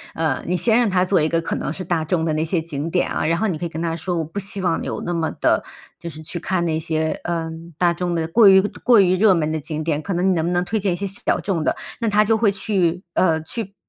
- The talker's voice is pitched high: No, medium, 175 Hz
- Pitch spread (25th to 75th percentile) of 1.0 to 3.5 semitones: Yes, average, 3.0 semitones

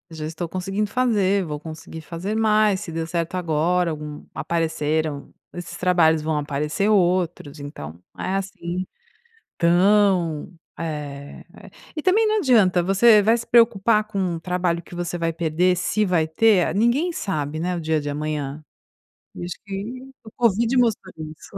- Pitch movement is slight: No, average, 4.3 semitones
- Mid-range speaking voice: Yes, medium, 175 Hz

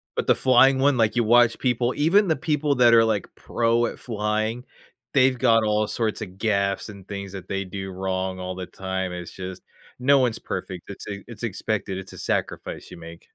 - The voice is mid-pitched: No, low, 110 Hz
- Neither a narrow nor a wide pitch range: Yes, average, 4.3 semitones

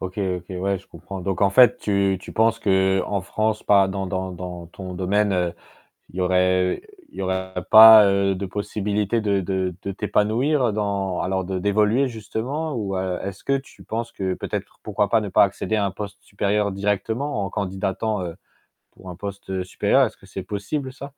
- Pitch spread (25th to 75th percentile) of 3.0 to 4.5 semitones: No, narrow, 2.4 semitones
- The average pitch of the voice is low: Yes, low, 100 Hz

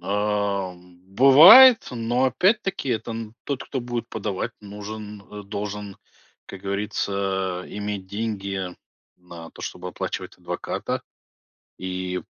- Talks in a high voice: No, low, 105 Hz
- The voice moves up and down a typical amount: Yes, average, 3.1 semitones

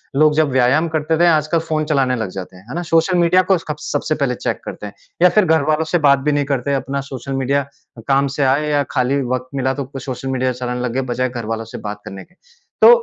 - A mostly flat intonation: No, average, 3.4 semitones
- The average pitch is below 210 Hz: Yes, medium, 140 Hz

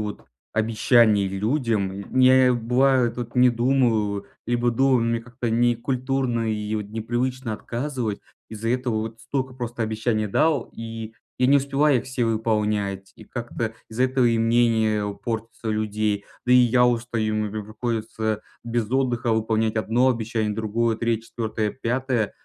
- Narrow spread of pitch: Yes, narrow, 2.3 semitones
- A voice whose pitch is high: No, low, 115 Hz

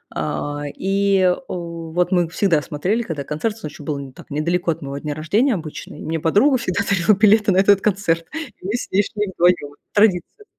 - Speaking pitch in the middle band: Yes, medium, 180 Hz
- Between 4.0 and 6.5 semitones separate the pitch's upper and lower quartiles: Yes, average, 4.7 semitones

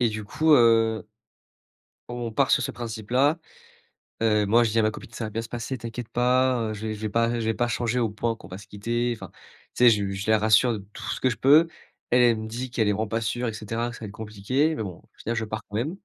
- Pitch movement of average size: No, narrow, 2.0 semitones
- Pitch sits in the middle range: No, low, 115 Hz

